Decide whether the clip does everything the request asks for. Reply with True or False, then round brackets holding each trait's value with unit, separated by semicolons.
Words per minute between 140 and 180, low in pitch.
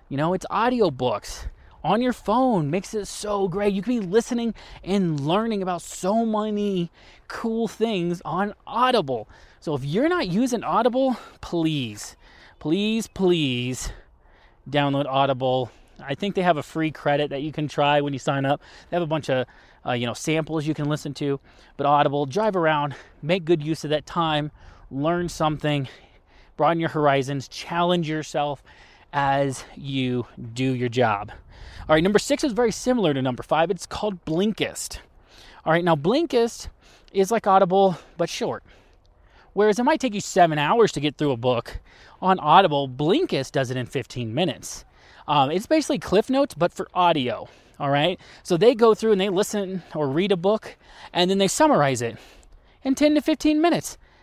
False (175 wpm; 165 Hz)